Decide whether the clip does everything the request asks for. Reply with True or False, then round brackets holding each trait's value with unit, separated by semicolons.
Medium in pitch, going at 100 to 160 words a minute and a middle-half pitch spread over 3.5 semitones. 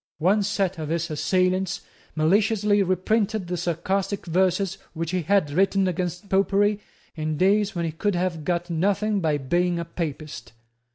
False (180 Hz; 155 wpm; 3.0 semitones)